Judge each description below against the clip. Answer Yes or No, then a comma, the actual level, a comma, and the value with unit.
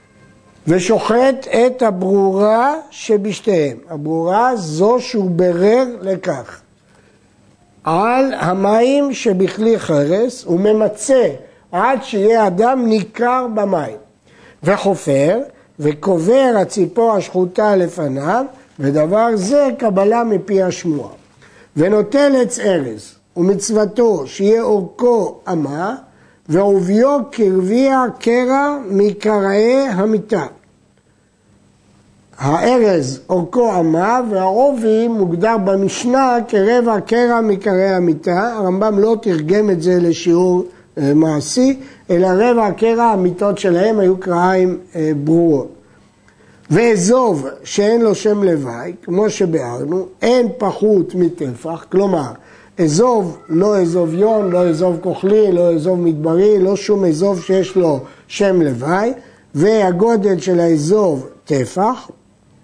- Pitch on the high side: Yes, high, 195 Hz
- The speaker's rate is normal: No, slow, 95 wpm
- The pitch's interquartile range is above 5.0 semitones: No, average, 4.4 semitones